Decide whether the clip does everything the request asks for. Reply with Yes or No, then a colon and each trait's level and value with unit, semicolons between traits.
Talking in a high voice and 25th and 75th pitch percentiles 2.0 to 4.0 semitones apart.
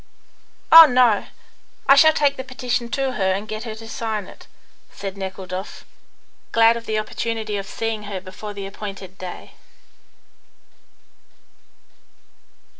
Yes: high, 215 Hz; average, 3.3 semitones